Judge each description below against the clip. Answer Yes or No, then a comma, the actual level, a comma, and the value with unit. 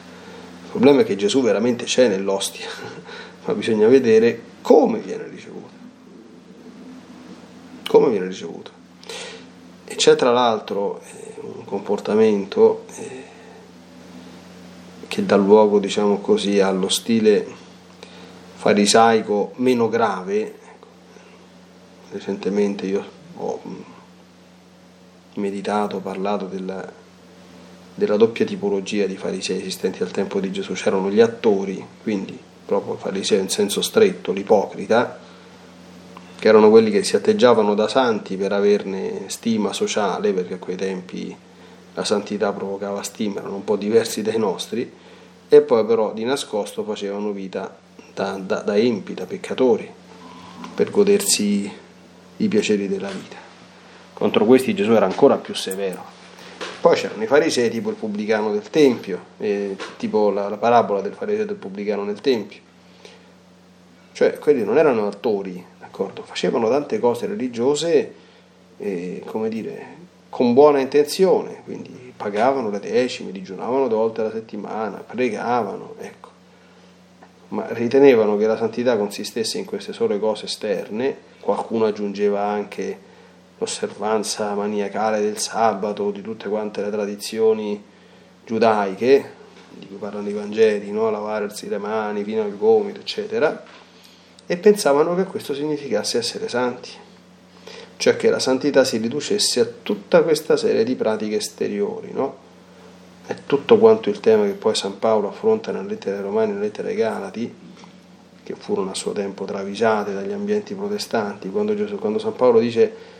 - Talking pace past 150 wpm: No, average, 135 wpm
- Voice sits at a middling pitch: No, low, 115 Hz